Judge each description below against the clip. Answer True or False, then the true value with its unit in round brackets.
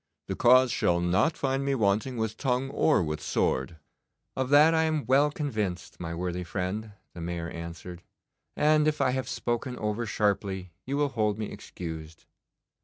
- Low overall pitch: True (110 Hz)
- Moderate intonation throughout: False (7.1 semitones)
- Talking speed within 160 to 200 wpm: True (170 wpm)